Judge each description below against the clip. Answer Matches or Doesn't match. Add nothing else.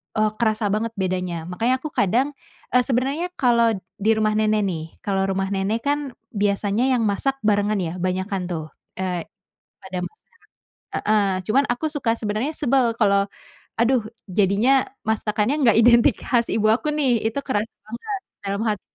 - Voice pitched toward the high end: Matches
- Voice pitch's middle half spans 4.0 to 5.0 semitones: Doesn't match